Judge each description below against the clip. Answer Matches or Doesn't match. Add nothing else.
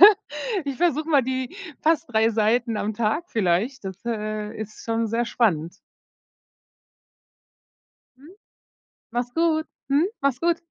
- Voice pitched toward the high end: Matches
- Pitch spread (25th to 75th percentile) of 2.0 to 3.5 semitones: Doesn't match